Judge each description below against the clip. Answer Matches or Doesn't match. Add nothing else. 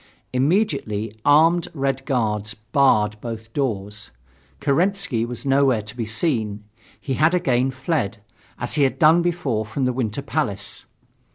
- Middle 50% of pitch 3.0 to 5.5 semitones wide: Matches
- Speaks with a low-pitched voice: Matches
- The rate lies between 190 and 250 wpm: Doesn't match